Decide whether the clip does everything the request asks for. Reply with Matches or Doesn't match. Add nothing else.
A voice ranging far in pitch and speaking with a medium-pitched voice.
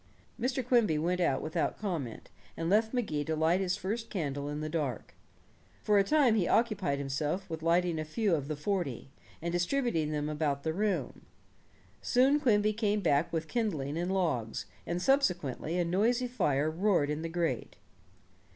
Matches